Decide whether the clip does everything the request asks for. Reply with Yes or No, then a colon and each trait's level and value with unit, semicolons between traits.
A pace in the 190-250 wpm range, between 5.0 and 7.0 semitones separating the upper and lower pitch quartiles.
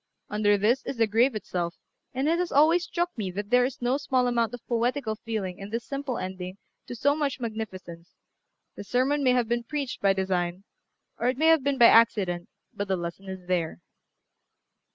Yes: average, 195 wpm; wide, 5.4 semitones